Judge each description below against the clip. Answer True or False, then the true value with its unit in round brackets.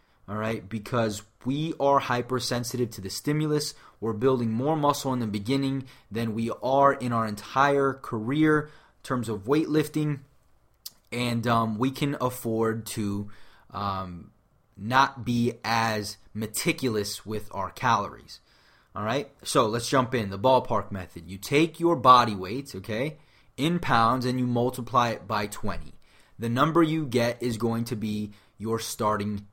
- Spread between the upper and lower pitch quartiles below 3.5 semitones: False (3.8 semitones)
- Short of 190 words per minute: True (150 wpm)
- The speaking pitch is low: True (120 Hz)